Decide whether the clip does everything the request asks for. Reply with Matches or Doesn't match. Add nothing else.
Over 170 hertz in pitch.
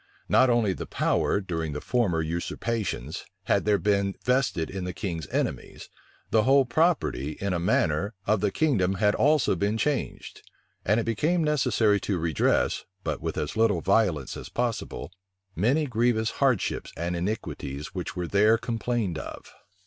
Doesn't match